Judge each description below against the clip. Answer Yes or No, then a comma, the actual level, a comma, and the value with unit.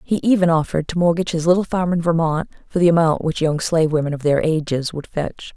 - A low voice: No, medium, 165 Hz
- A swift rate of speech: Yes, fast, 235 wpm